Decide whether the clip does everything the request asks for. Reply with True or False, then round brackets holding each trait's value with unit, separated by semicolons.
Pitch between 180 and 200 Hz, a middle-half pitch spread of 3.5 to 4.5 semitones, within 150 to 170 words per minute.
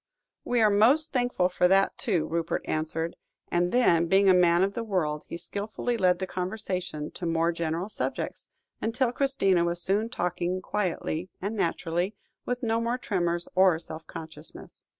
True (185 Hz; 4.2 semitones; 165 wpm)